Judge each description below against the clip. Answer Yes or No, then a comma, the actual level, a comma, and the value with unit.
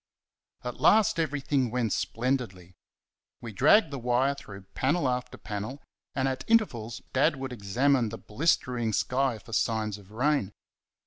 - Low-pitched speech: Yes, low, 125 Hz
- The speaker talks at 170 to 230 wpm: No, average, 140 wpm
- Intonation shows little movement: No, average, 3.9 semitones